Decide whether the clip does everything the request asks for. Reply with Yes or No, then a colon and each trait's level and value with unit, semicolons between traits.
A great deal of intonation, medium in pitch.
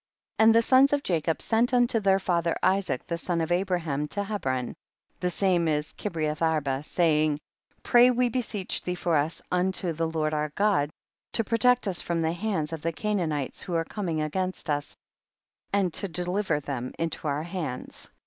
No: average, 4.5 semitones; medium, 175 Hz